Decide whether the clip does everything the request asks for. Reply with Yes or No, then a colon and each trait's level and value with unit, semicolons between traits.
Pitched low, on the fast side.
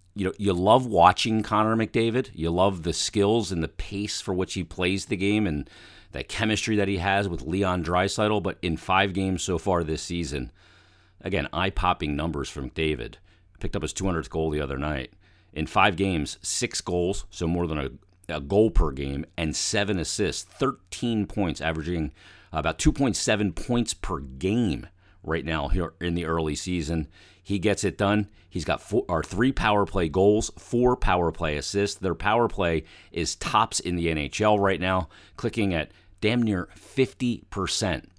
No: very low, 95 Hz; average, 175 wpm